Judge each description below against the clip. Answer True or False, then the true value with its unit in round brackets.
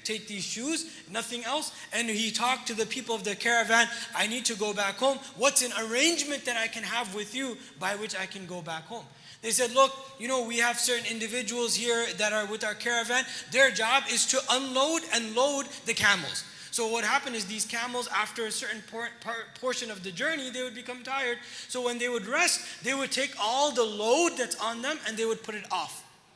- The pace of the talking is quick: True (225 wpm)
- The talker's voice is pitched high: True (235 Hz)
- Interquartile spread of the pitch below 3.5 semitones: True (2.9 semitones)